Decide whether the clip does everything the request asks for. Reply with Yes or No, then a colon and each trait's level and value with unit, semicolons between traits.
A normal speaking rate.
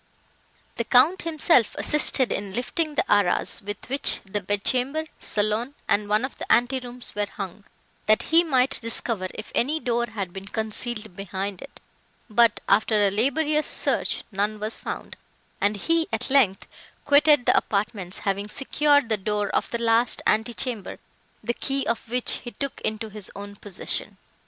Yes: average, 165 wpm